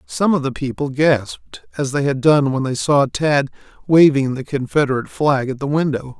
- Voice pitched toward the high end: No, medium, 140 Hz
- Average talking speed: Yes, average, 195 wpm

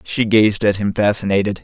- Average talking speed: Yes, average, 185 wpm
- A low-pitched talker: Yes, low, 105 Hz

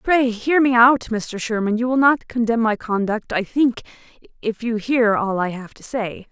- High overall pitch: Yes, high, 230 Hz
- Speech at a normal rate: No, fast, 210 wpm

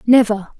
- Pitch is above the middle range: Yes, high, 220 Hz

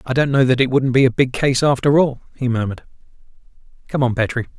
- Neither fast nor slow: No, fast, 220 wpm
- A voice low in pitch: Yes, low, 130 Hz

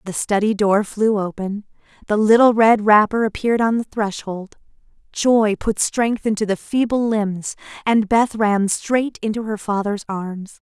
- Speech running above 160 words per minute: No, average, 155 wpm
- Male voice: No, female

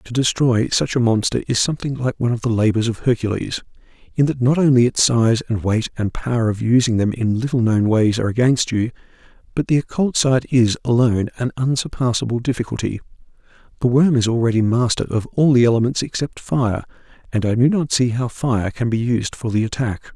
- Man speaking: Yes, male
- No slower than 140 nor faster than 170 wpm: No, average, 195 wpm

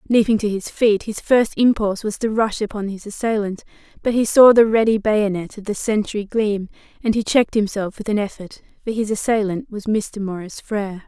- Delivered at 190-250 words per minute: Yes, average, 200 wpm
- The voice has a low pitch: No, high, 210 Hz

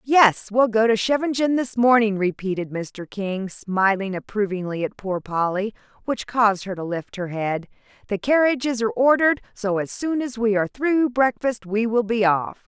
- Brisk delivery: No, average, 180 wpm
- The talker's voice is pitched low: No, high, 220 Hz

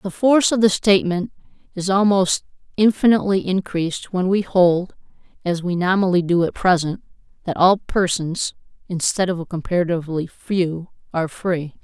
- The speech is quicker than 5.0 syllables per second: Yes, 5.2 syllables/s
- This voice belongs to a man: No, female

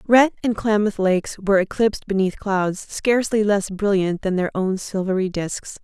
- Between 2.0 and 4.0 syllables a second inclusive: No, 5.1 syllables/s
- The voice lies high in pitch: Yes, high, 200 Hz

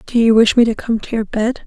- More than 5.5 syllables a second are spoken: Yes, 6.0 syllables/s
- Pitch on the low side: No, high, 225 Hz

